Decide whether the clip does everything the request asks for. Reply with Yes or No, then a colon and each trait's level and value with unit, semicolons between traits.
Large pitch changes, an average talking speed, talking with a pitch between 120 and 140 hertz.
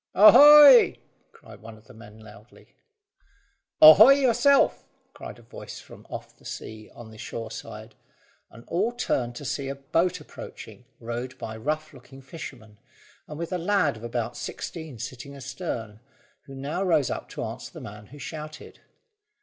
Yes: wide, 6.7 semitones; average, 165 wpm; low, 135 Hz